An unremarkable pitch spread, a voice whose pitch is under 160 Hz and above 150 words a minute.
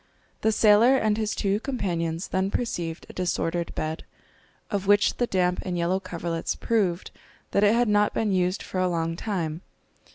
No: average, 3.4 semitones; high, 190 Hz; average, 170 wpm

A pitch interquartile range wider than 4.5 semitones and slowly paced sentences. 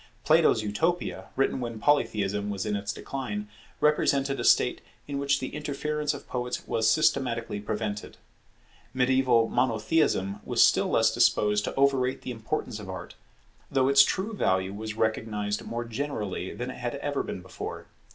No: average, 4.9 semitones; average, 155 wpm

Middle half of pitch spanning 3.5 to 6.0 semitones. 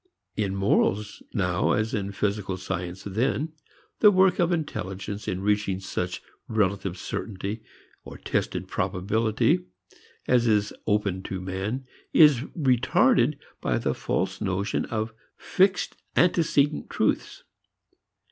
Yes: average, 4.7 semitones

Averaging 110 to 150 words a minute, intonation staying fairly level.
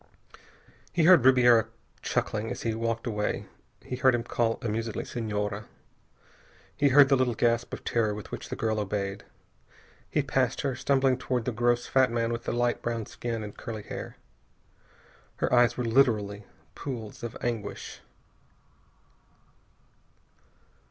Yes: average, 145 wpm; narrow, 2.3 semitones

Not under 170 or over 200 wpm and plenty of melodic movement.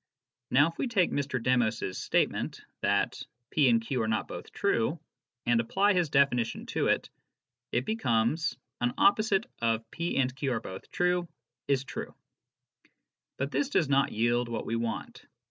Yes: average, 180 wpm; wide, 6.1 semitones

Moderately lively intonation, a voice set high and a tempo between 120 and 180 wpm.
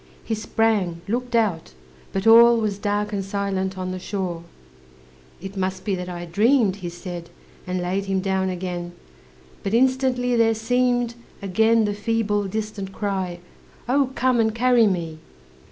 Yes: average, 3.6 semitones; high, 200 Hz; average, 155 wpm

